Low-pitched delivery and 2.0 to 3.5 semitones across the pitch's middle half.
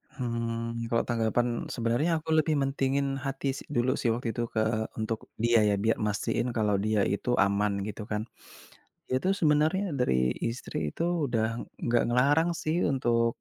No: low, 120 Hz; average, 4.0 semitones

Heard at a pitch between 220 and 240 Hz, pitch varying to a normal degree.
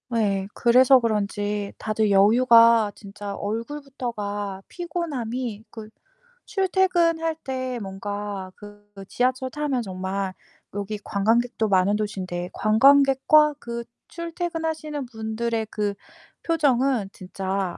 Yes: high, 225 Hz; average, 4.9 semitones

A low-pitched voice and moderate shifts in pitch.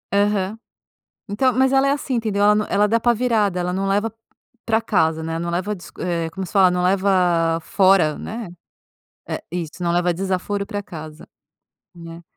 No: high, 190 Hz; average, 3.3 semitones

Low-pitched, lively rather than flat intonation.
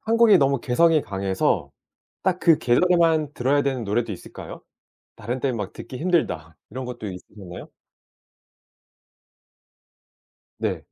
Yes: low, 130 Hz; wide, 7.8 semitones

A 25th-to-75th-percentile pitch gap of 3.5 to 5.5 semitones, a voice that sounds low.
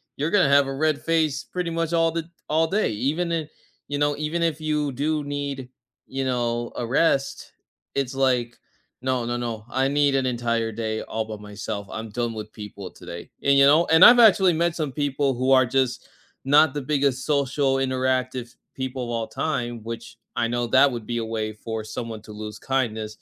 Yes: average, 4.0 semitones; low, 130 Hz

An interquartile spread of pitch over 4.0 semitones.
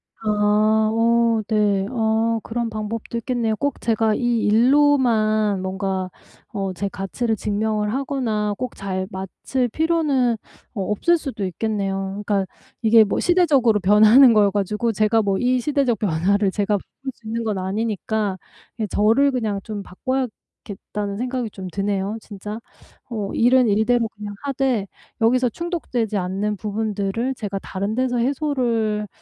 No: average, 3.1 semitones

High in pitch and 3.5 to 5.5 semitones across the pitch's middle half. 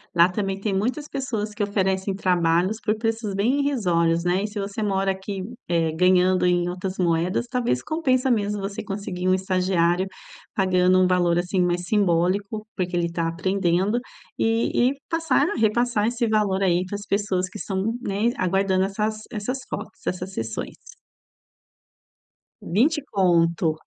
No: high, 195 Hz; average, 2.9 semitones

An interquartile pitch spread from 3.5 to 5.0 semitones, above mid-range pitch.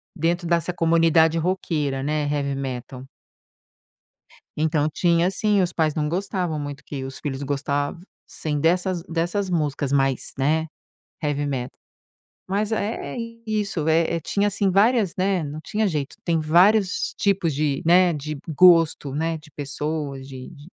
No: average, 3.9 semitones; medium, 160 Hz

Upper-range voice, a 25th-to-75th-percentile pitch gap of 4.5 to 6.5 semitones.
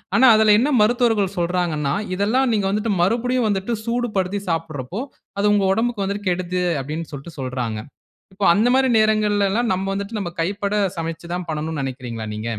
Yes: high, 195 Hz; average, 4.8 semitones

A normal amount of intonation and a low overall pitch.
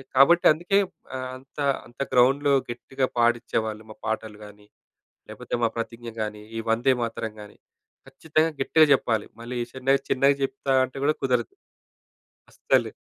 Yes: average, 3.2 semitones; low, 125 Hz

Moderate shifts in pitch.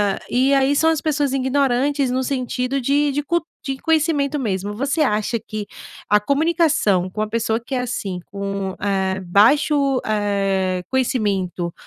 No: wide, 5.7 semitones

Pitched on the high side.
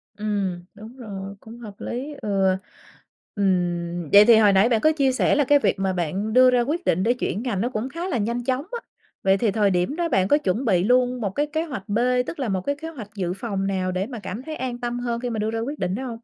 Yes: high, 225 Hz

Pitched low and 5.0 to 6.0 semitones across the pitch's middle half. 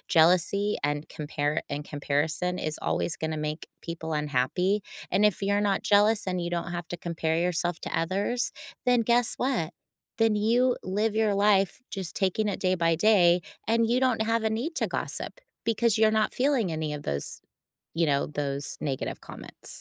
No: medium, 185 Hz; average, 5.3 semitones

